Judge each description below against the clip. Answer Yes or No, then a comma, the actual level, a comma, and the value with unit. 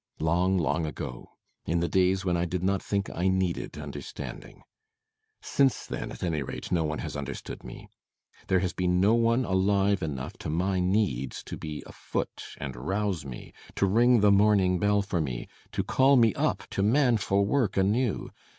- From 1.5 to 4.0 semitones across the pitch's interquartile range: Yes, average, 3.4 semitones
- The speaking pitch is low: Yes, very low, 95 Hz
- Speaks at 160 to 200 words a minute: Yes, average, 180 wpm